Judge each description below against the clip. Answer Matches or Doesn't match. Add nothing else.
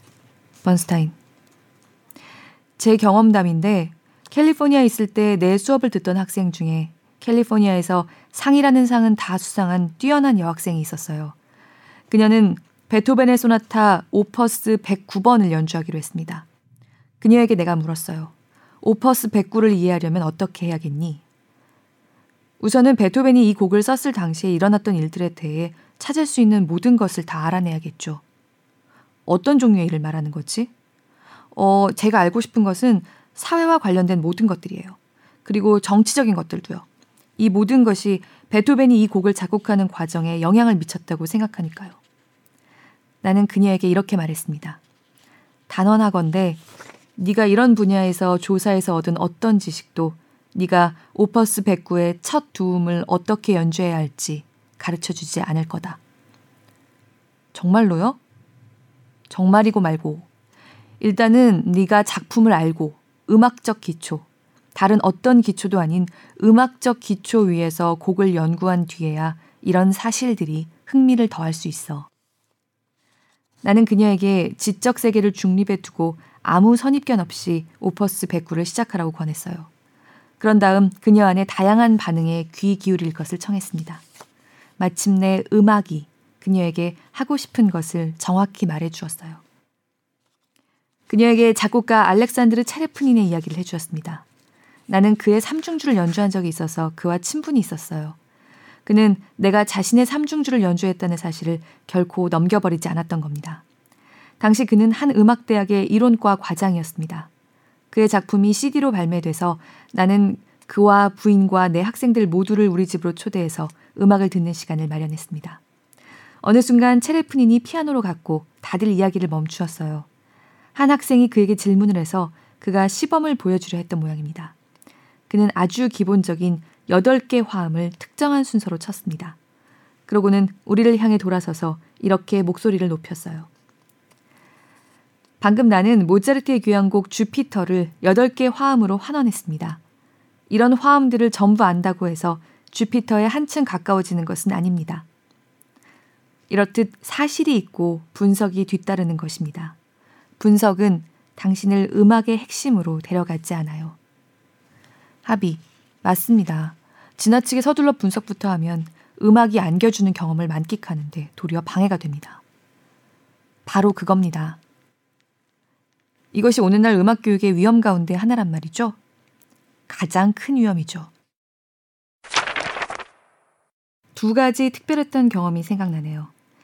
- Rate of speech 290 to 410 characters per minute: Matches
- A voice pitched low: Doesn't match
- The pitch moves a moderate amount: Matches